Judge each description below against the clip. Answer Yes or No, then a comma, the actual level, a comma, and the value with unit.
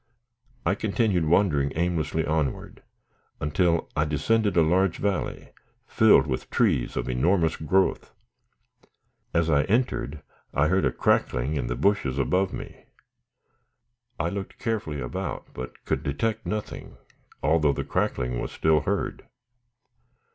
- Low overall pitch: Yes, very low, 80 Hz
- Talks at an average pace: No, slow, 125 wpm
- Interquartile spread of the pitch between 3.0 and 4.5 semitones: No, average, 5.3 semitones